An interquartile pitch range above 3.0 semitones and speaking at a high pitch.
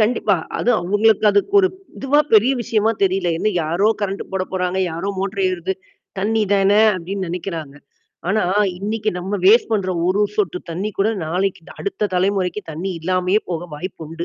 No: average, 2.7 semitones; high, 195 Hz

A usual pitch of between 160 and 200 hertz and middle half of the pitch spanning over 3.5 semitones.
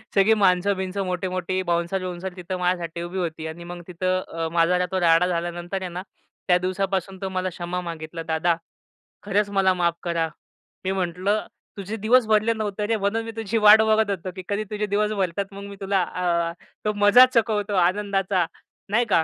No: medium, 185 Hz; average, 2.7 semitones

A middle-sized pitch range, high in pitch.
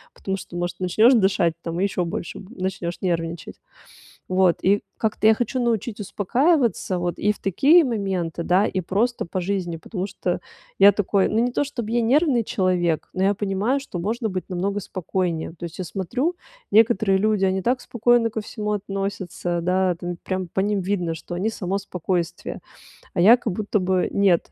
Yes: average, 3.5 semitones; high, 195 Hz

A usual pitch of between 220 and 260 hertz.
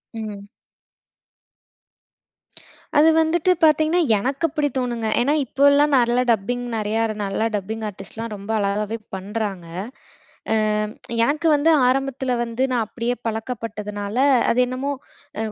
Yes: high, 230 Hz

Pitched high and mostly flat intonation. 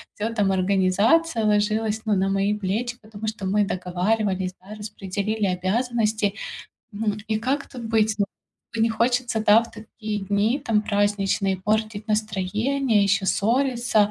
Yes: high, 210 Hz; narrow, 2.1 semitones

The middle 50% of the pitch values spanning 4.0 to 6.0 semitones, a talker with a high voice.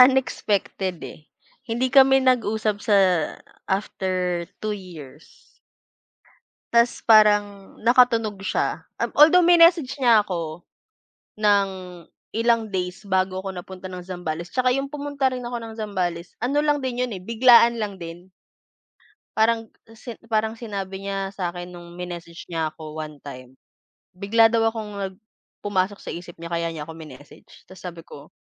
Yes: average, 4.8 semitones; high, 200 Hz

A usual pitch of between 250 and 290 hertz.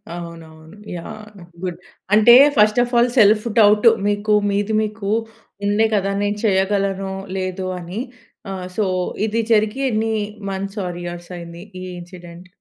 No: high, 200 Hz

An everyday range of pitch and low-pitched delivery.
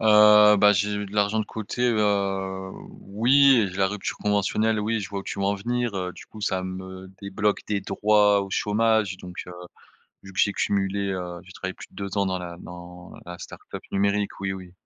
No: narrow, 1.9 semitones; low, 100 Hz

